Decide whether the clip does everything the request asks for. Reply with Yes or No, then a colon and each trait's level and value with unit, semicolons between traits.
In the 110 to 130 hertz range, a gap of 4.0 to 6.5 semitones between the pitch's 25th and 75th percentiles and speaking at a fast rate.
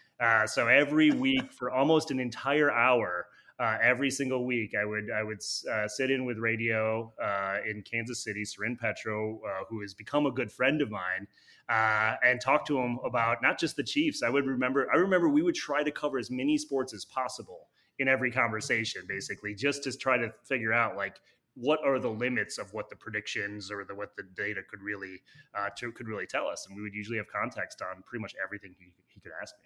Yes: low, 120 Hz; average, 4.3 semitones; fast, 220 wpm